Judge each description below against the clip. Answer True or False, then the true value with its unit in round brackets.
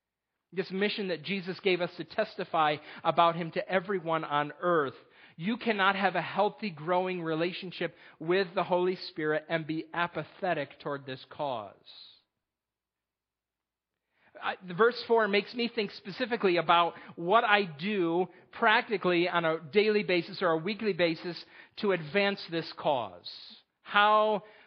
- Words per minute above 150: False (135 wpm)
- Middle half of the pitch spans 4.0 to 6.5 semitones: False (3.4 semitones)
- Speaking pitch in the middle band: True (180 Hz)